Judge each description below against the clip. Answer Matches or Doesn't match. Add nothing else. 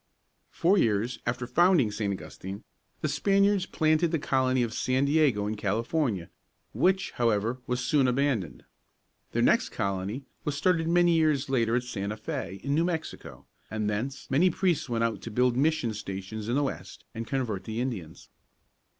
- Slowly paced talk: Doesn't match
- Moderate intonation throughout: Doesn't match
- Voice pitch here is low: Matches